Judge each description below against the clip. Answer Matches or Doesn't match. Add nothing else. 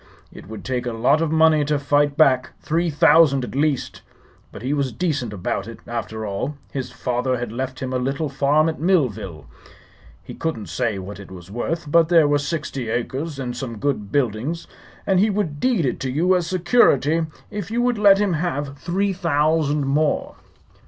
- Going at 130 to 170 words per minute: Doesn't match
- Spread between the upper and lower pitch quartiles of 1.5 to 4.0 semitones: Doesn't match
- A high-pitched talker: Doesn't match